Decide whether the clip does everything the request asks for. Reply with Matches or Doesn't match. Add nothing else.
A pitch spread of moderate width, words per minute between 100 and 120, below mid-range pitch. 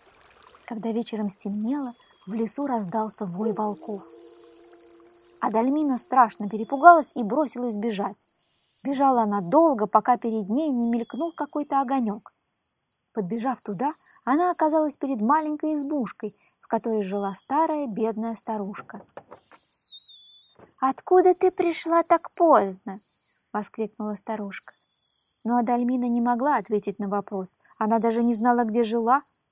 Doesn't match